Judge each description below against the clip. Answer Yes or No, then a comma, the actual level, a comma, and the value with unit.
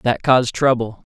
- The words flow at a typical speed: Yes, average, 155 wpm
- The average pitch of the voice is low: Yes, low, 120 Hz